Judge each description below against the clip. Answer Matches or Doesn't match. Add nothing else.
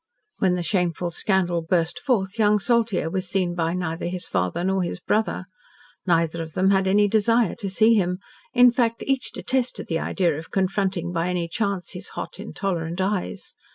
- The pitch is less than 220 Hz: Matches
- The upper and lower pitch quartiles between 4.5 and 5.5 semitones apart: Doesn't match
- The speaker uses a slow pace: Doesn't match